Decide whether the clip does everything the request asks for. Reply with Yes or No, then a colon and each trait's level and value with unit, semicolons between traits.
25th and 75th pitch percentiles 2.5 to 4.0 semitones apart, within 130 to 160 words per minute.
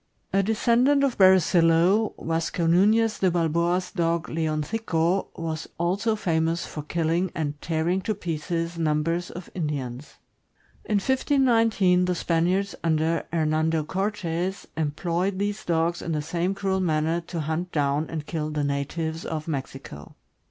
Yes: average, 3.0 semitones; average, 145 wpm